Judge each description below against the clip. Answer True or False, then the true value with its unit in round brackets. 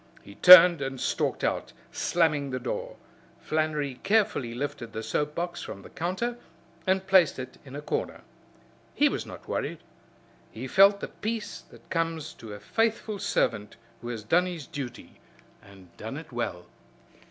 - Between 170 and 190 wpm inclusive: False (160 wpm)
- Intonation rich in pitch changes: True (7.1 semitones)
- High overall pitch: False (150 Hz)